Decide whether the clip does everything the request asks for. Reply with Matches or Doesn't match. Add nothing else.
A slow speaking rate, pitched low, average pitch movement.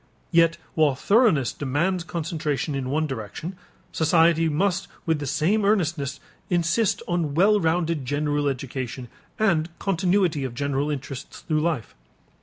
Doesn't match